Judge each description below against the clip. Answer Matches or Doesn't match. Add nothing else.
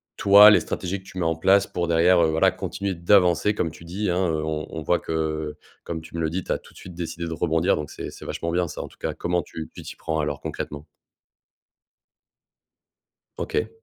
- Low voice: Matches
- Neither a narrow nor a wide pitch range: Doesn't match